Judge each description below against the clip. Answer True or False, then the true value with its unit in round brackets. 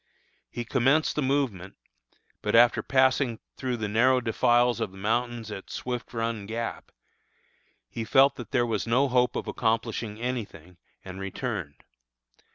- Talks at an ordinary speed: True (150 wpm)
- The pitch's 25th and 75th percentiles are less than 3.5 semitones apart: True (2.6 semitones)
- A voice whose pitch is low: True (120 Hz)